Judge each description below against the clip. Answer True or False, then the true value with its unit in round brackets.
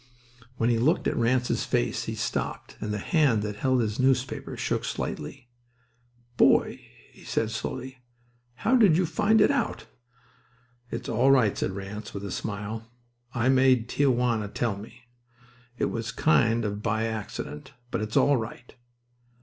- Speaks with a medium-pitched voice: False (115 Hz)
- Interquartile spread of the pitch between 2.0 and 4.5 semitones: True (3.6 semitones)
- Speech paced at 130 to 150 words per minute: False (160 wpm)